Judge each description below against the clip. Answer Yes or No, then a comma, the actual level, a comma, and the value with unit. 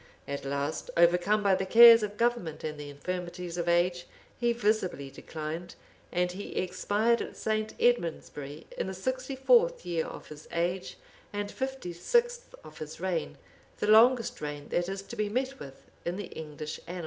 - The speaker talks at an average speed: Yes, average, 170 wpm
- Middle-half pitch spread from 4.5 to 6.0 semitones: Yes, wide, 5.5 semitones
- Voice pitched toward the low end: No, medium, 185 Hz